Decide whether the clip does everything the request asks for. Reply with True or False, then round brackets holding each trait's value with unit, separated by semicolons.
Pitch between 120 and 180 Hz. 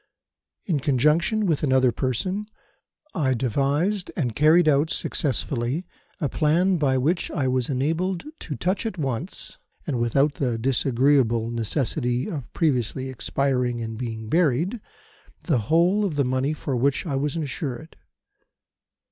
True (140 Hz)